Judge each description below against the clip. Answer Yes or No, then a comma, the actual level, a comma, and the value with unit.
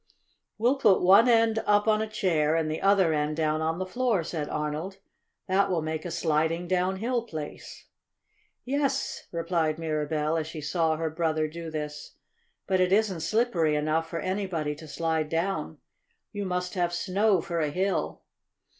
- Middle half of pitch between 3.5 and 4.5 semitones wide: Yes, average, 3.8 semitones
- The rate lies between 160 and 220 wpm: Yes, average, 165 wpm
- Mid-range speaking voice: Yes, medium, 170 Hz